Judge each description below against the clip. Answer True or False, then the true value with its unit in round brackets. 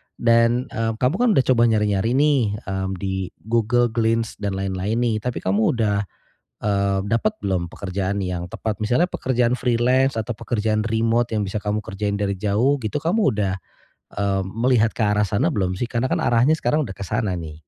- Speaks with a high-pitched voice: False (110 Hz)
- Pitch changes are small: False (3.5 semitones)